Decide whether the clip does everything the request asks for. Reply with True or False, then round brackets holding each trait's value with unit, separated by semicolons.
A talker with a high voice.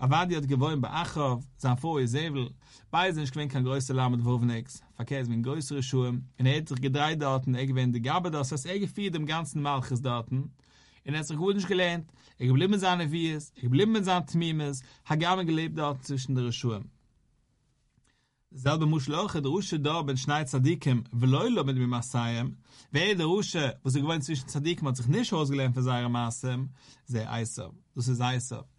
False (135 Hz)